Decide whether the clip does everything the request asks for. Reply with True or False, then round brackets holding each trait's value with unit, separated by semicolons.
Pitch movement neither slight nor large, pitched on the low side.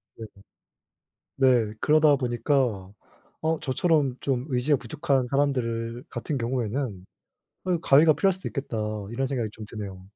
True (3.8 semitones; 130 Hz)